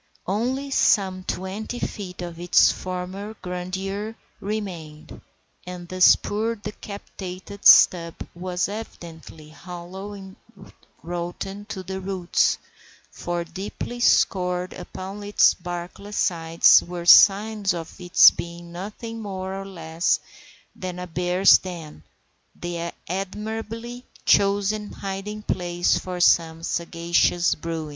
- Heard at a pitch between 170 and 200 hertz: Yes, medium, 185 Hz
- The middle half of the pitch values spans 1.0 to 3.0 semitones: Yes, average, 2.7 semitones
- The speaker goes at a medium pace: No, slow, 110 wpm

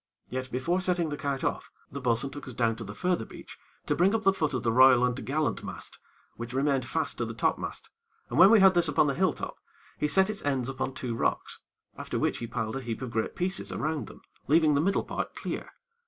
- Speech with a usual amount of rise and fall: No, wide, 5.7 semitones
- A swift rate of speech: Yes, fast, 240 wpm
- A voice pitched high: No, medium, 140 Hz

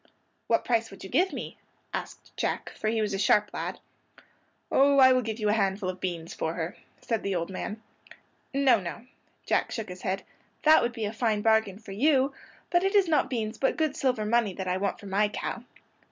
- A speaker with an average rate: No, fast, 215 wpm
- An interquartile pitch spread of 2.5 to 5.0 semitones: Yes, average, 4.6 semitones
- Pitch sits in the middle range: No, high, 220 Hz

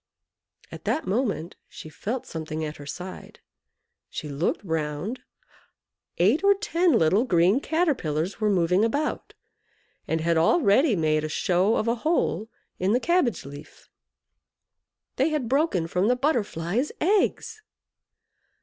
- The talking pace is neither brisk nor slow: No, slow, 130 wpm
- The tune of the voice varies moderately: No, wide, 8.8 semitones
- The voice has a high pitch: Yes, high, 205 Hz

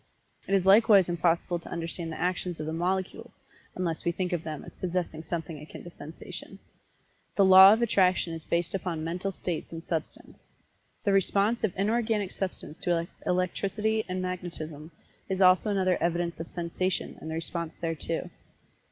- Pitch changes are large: No, narrow, 2.4 semitones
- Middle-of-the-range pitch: Yes, medium, 180 Hz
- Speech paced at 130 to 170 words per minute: Yes, average, 165 wpm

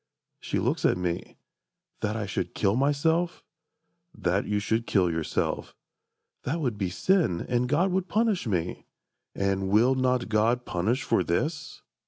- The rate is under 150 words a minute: Yes, average, 140 wpm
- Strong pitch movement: Yes, wide, 6.7 semitones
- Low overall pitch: Yes, low, 115 Hz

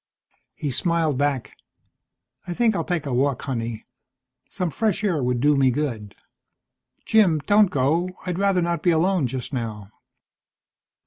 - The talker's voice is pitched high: No, medium, 150 Hz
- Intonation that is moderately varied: No, wide, 5.9 semitones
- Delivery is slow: No, average, 145 wpm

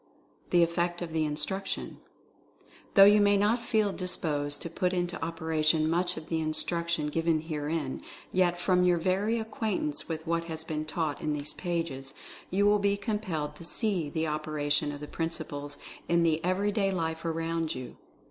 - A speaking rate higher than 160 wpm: Yes, average, 175 wpm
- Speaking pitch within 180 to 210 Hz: No, medium, 165 Hz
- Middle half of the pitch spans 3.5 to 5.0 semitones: No, average, 3.0 semitones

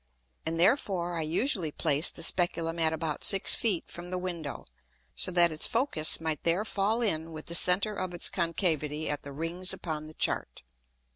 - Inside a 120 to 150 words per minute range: No, average, 185 wpm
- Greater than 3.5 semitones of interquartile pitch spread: No, narrow, 2.6 semitones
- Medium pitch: Yes, medium, 170 Hz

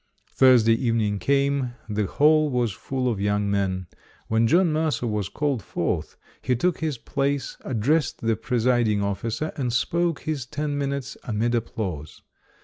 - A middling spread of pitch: Yes, average, 4.7 semitones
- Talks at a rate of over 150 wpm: No, average, 145 wpm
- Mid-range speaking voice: No, low, 125 Hz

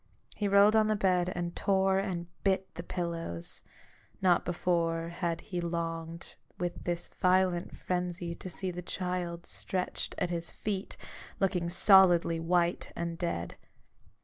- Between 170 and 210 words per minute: No, average, 140 wpm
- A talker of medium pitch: Yes, medium, 175 Hz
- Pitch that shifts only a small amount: Yes, narrow, 1.8 semitones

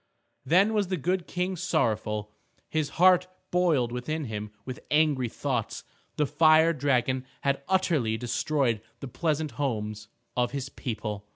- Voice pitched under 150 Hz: Yes, medium, 140 Hz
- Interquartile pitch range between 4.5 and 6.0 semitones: Yes, wide, 5.6 semitones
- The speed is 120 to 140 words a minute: Yes, slow, 135 wpm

